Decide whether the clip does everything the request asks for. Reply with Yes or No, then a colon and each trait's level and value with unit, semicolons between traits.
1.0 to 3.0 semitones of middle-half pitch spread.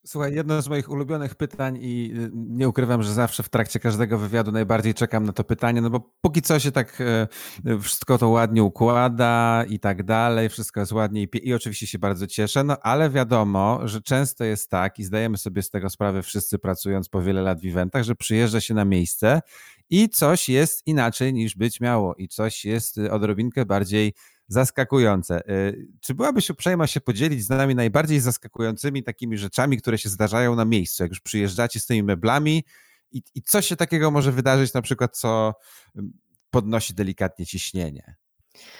No: average, 3.8 semitones